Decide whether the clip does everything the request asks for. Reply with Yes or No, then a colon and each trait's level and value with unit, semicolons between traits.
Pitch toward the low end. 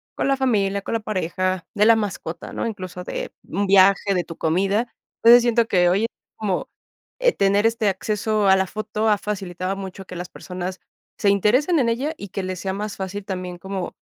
No: high, 200 Hz